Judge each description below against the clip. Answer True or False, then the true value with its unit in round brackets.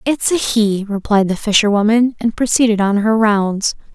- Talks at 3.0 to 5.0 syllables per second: True (4.7 syllables/s)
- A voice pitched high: True (215 Hz)